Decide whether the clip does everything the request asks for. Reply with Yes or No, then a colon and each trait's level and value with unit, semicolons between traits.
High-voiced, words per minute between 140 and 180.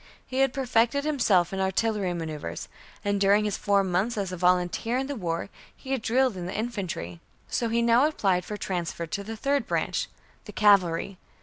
No: high, 205 Hz; average, 190 wpm